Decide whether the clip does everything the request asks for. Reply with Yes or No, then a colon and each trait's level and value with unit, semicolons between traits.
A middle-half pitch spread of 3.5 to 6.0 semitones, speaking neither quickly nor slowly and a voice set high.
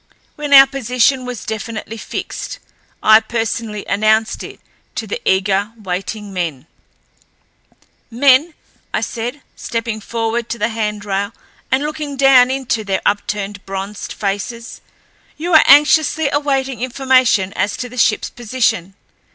No: average, 4.3 semitones; slow, 125 wpm; high, 230 Hz